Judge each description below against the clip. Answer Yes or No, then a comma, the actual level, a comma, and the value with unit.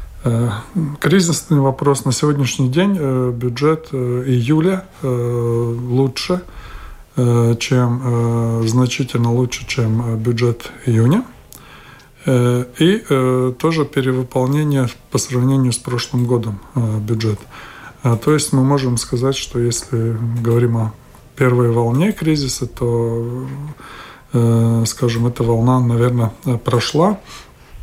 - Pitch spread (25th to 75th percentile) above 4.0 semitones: No, narrow, 2.4 semitones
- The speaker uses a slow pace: Yes, slow, 90 wpm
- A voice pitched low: Yes, low, 125 Hz